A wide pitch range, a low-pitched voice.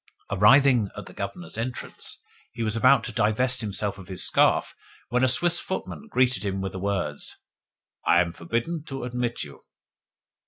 No: average, 4.5 semitones; low, 115 Hz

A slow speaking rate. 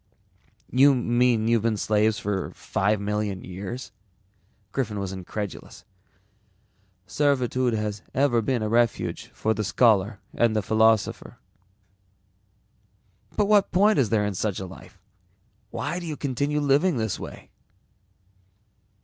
Yes: slow, 125 wpm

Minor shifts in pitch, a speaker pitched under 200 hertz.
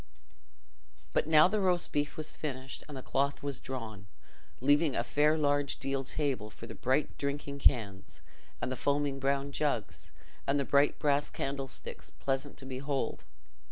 Yes: narrow, 1.7 semitones; medium, 140 Hz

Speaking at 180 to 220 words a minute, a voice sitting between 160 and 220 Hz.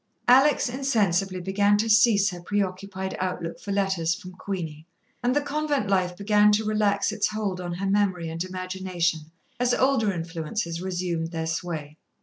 No: average, 155 wpm; high, 190 Hz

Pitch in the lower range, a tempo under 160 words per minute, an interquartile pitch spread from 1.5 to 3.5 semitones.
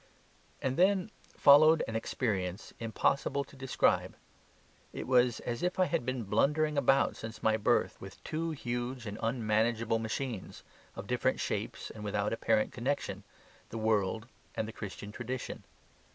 No: low, 120 Hz; average, 145 wpm; average, 4.0 semitones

